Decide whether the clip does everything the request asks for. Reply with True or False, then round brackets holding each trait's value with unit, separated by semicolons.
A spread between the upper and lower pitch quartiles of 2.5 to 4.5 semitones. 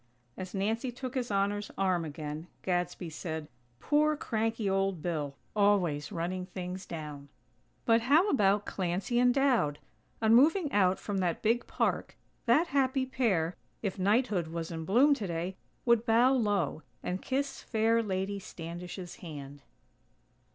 False (5.5 semitones)